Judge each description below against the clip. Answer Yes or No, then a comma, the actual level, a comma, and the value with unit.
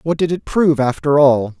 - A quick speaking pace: Yes, fast, 225 wpm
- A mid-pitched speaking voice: Yes, medium, 145 Hz